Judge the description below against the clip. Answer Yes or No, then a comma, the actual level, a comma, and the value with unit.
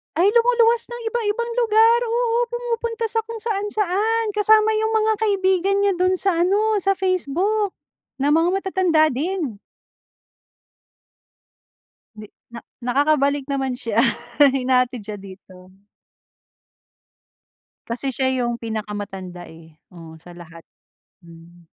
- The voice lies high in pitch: Yes, very high, 360 Hz